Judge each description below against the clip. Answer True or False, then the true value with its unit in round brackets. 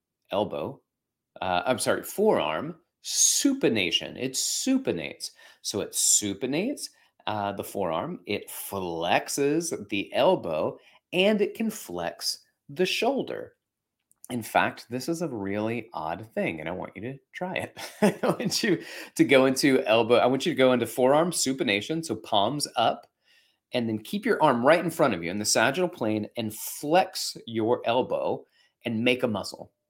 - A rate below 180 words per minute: True (160 wpm)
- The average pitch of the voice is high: False (135 Hz)